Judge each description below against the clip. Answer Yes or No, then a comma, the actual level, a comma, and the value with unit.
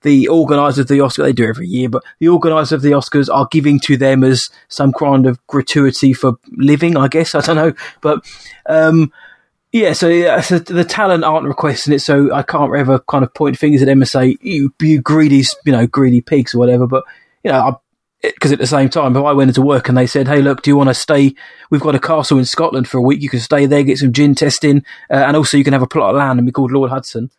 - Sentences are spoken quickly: Yes, fast, 250 wpm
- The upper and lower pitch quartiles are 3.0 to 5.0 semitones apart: No, narrow, 2.6 semitones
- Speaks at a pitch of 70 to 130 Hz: No, medium, 140 Hz